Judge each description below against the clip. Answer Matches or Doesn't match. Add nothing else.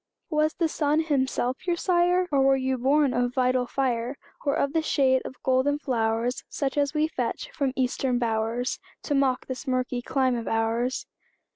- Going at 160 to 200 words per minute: Matches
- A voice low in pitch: Doesn't match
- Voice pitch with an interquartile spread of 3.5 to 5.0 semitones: Doesn't match